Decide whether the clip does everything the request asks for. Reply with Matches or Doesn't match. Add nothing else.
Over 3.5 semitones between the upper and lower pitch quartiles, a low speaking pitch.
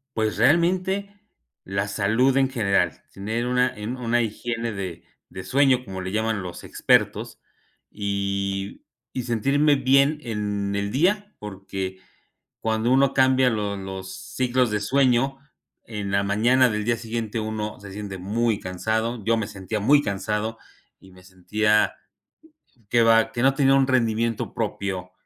Matches